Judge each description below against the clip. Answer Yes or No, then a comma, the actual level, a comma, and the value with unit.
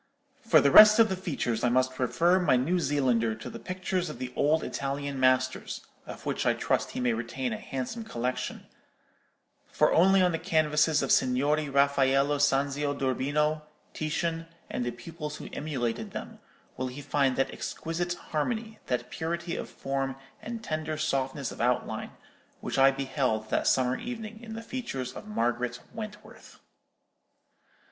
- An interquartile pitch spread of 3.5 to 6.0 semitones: Yes, average, 4.8 semitones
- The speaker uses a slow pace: No, average, 155 wpm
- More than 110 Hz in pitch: Yes, medium, 140 Hz